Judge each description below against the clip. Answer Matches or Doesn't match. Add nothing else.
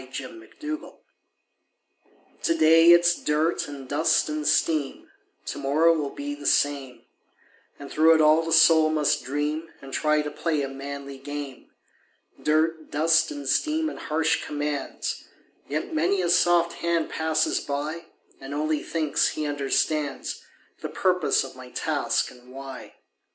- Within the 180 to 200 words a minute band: Doesn't match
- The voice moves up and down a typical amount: Doesn't match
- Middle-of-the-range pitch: Matches